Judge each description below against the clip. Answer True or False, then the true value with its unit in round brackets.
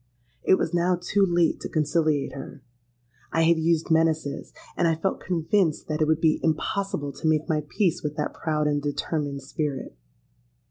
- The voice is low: False (160 Hz)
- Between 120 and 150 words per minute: False (175 wpm)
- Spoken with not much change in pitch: True (2.1 semitones)